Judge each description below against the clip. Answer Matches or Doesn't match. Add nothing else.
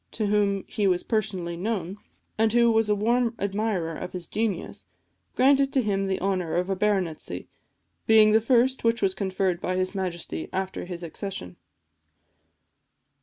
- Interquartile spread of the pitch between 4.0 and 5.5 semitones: Doesn't match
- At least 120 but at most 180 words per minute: Matches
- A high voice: Matches